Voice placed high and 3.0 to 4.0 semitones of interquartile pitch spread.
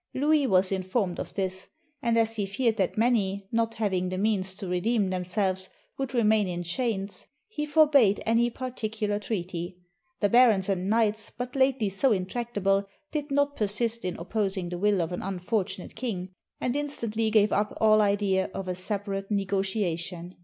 Yes: high, 205 Hz; average, 3.5 semitones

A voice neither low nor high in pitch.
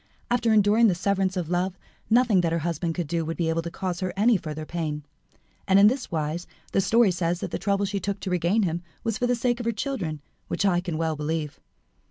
Yes: medium, 180 Hz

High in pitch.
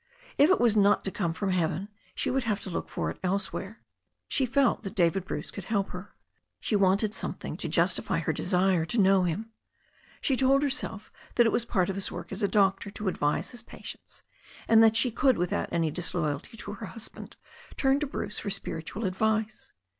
Yes: high, 200 Hz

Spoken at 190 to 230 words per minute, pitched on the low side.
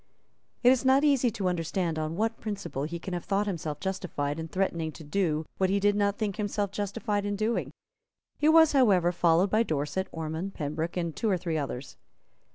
No: average, 195 wpm; high, 190 Hz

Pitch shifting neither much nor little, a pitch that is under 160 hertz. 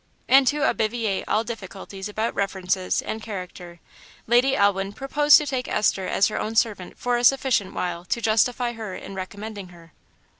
No: average, 4.0 semitones; high, 215 Hz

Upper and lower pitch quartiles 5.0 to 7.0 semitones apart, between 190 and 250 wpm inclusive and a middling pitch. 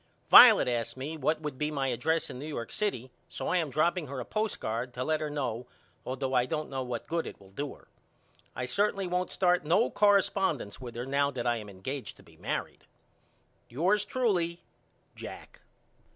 Yes: average, 5.3 semitones; average, 195 wpm; medium, 145 Hz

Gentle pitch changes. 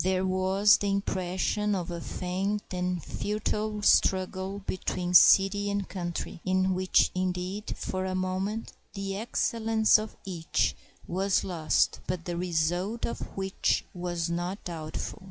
Yes: narrow, 2.0 semitones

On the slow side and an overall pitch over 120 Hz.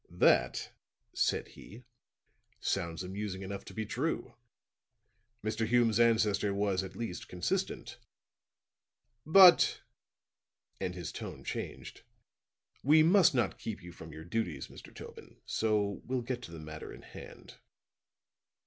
No: slow, 130 wpm; low, 105 Hz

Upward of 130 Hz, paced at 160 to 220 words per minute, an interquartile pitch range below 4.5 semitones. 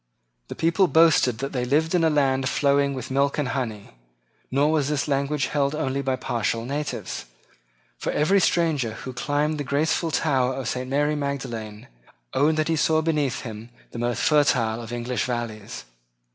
Yes: medium, 140 Hz; average, 170 wpm; average, 3.4 semitones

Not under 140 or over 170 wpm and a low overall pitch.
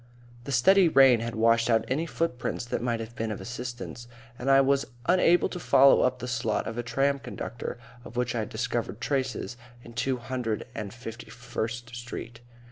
No: average, 190 wpm; low, 120 Hz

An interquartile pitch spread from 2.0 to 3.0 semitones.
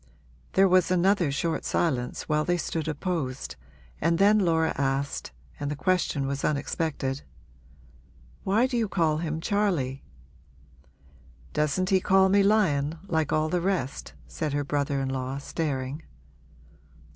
No: average, 4.6 semitones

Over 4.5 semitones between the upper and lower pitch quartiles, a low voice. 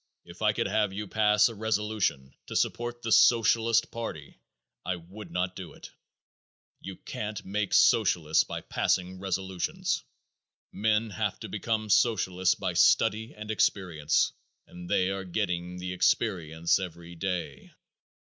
No: average, 3.3 semitones; very low, 95 Hz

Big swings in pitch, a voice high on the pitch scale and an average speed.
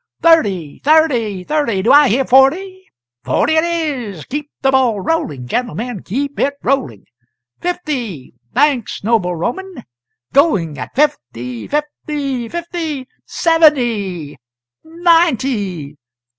No: wide, 7.8 semitones; very high, 265 Hz; slow, 105 wpm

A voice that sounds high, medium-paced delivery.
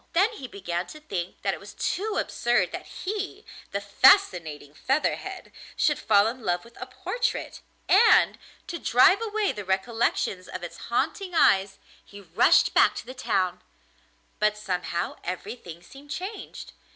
Yes: high, 225 Hz; average, 150 wpm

